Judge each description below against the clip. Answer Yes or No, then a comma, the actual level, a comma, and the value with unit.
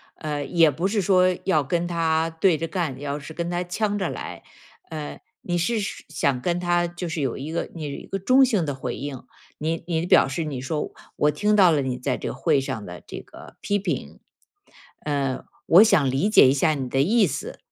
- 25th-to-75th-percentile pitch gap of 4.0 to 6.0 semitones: Yes, average, 4.3 semitones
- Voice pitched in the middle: Yes, medium, 160 Hz